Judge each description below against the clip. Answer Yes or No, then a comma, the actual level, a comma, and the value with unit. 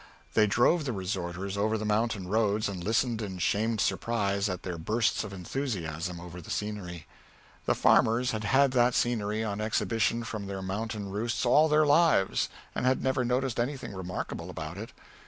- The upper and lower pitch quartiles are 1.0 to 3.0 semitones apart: No, average, 3.8 semitones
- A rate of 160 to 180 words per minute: Yes, average, 175 wpm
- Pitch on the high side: No, low, 105 Hz